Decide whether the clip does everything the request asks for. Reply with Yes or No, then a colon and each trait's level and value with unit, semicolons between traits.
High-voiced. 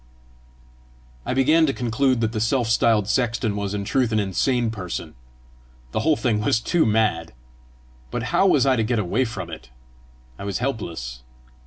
No: low, 110 Hz